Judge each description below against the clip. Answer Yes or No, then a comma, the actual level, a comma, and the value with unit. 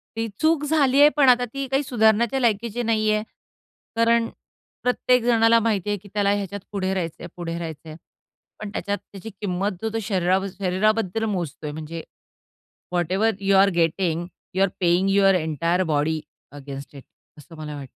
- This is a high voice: Yes, high, 200 Hz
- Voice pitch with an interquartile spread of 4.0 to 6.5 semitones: Yes, average, 4.7 semitones